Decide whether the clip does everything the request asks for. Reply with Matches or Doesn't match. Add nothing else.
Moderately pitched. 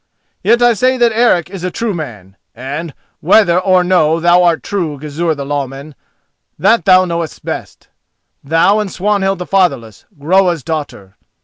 Matches